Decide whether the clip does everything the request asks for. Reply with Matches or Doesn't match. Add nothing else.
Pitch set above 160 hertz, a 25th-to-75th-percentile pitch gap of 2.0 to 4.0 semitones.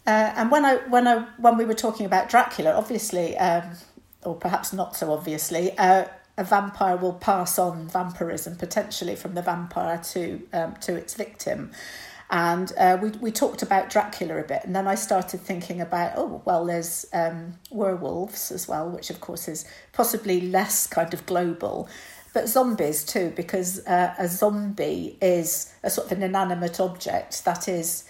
Matches